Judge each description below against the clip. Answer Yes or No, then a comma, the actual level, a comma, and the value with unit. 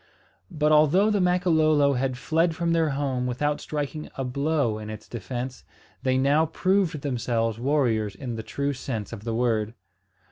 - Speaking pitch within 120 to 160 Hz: Yes, medium, 140 Hz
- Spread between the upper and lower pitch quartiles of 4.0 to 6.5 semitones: Yes, average, 4.6 semitones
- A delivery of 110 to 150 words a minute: No, average, 165 wpm